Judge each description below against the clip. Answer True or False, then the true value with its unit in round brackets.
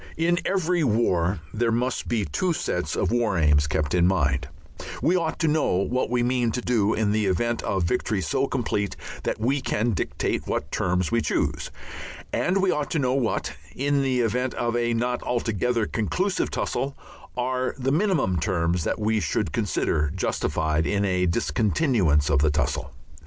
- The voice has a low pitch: True (115 Hz)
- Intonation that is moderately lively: False (6.2 semitones)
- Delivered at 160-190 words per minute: True (180 wpm)